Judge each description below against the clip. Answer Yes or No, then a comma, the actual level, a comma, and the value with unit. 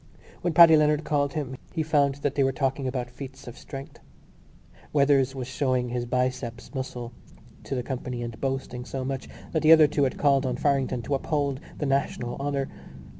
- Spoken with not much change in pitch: Yes, narrow, 2.1 semitones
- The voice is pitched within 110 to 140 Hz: Yes, low, 135 Hz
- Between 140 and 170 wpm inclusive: No, average, 185 wpm